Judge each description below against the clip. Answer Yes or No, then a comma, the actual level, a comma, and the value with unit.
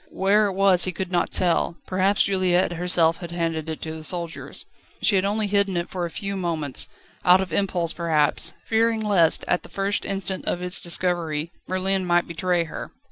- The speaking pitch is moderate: Yes, medium, 180 Hz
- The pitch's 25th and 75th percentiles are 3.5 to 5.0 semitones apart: No, narrow, 2.4 semitones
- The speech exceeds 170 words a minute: Yes, average, 190 wpm